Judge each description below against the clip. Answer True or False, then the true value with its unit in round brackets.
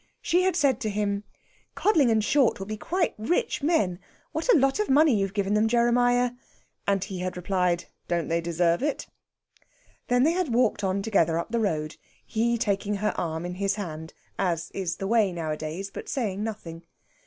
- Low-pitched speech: False (205 Hz)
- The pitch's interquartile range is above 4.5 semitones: True (5.4 semitones)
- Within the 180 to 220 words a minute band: True (190 wpm)